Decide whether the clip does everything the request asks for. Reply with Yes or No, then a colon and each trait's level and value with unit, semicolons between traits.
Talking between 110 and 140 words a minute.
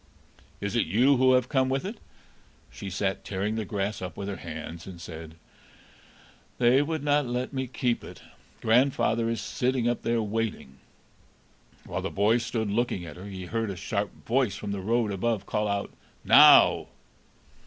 No: average, 175 wpm